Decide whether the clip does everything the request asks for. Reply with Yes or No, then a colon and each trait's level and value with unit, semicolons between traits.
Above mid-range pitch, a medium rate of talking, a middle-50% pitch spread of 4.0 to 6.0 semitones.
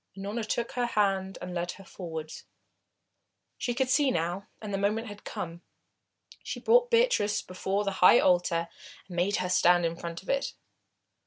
Yes: high, 195 Hz; average, 170 wpm; average, 4.3 semitones